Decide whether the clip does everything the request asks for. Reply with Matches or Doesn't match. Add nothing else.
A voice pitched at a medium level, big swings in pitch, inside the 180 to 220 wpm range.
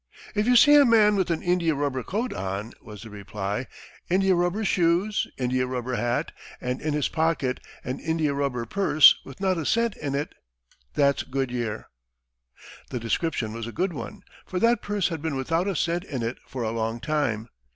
Matches